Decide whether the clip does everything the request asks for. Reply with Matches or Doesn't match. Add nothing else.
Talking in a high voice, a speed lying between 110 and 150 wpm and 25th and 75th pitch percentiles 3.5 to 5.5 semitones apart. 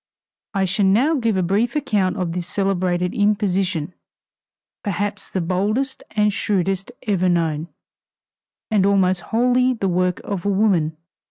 Doesn't match